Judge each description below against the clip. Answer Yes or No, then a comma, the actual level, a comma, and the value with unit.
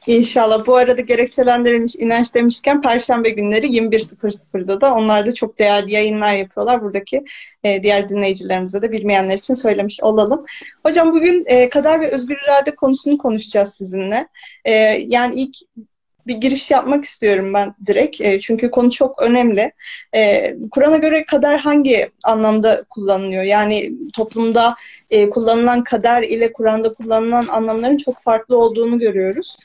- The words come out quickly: No, average, 130 wpm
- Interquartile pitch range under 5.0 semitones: Yes, average, 3.9 semitones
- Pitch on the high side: Yes, high, 235 Hz